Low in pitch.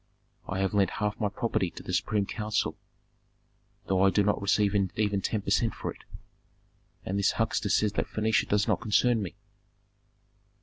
Yes: low, 105 Hz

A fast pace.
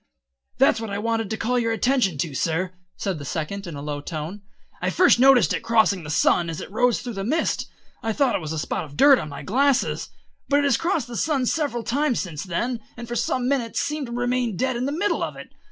Yes: fast, 245 wpm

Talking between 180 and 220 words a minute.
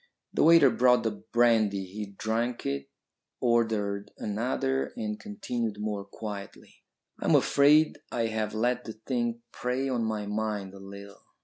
No: average, 145 wpm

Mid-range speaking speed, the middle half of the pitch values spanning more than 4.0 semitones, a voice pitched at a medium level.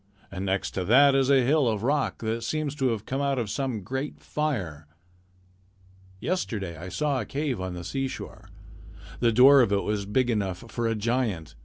No: average, 190 wpm; wide, 5.4 semitones; low, 120 Hz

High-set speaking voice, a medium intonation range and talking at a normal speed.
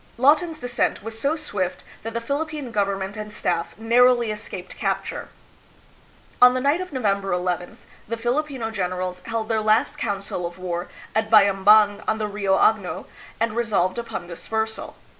Yes: high, 220 Hz; average, 3.5 semitones; average, 160 wpm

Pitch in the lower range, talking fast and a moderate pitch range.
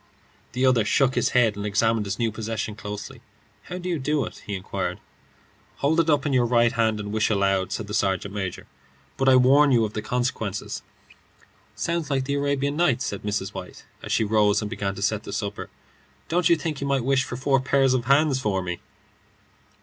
Yes: low, 120 Hz; fast, 210 wpm; average, 4.9 semitones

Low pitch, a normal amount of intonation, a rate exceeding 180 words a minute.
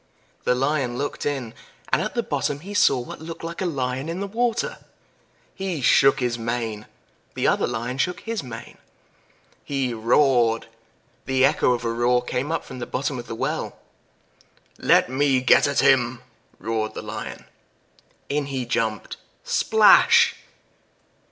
No: low, 130 Hz; average, 3.5 semitones; average, 155 wpm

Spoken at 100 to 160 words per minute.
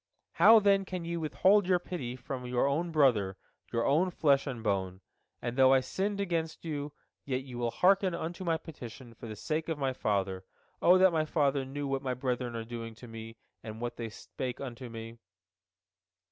No: average, 195 wpm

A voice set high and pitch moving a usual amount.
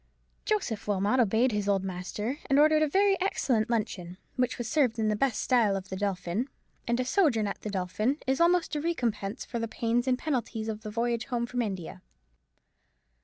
Yes: high, 230 Hz; average, 4.3 semitones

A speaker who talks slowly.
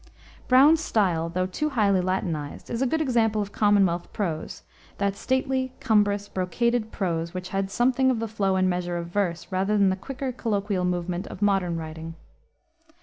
No: average, 170 wpm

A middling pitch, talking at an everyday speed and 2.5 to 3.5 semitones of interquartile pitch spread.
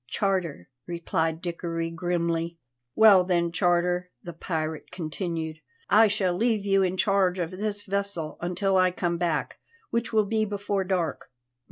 Yes: medium, 180 Hz; average, 145 wpm; average, 2.9 semitones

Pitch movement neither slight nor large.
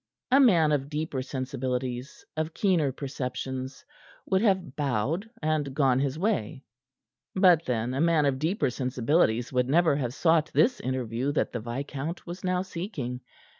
Yes: average, 4.6 semitones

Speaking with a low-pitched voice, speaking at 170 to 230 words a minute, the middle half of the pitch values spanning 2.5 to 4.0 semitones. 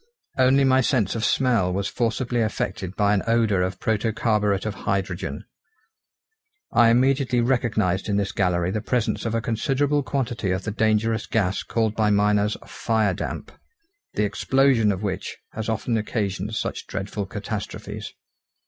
No: low, 110 Hz; average, 145 wpm; average, 2.9 semitones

